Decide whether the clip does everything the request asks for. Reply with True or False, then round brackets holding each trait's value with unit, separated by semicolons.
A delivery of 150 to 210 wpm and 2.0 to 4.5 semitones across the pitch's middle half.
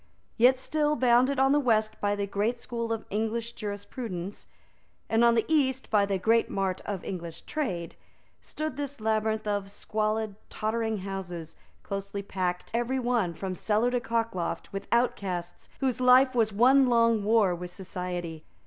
True (160 wpm; 3.7 semitones)